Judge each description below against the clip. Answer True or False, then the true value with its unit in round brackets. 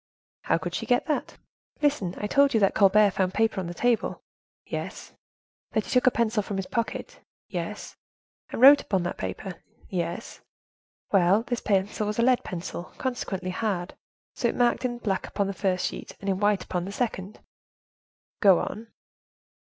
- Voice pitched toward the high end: True (205 Hz)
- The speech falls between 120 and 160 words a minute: False (175 wpm)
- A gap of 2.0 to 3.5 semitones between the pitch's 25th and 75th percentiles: False (3.9 semitones)